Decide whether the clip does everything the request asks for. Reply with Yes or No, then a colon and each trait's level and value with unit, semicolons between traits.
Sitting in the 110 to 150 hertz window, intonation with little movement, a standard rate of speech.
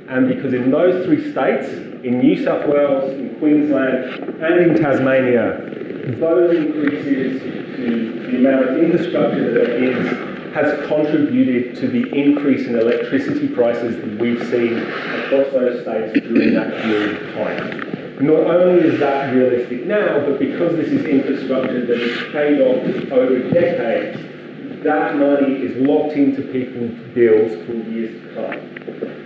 No: low, 135 Hz; average, 3.6 semitones; average, 150 wpm